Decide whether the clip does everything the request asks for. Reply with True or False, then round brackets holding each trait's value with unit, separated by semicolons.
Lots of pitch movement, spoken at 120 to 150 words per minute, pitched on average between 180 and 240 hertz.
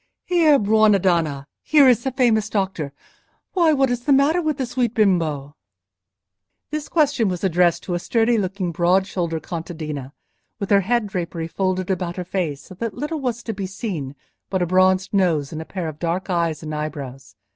False (5.8 semitones; 190 wpm; 190 Hz)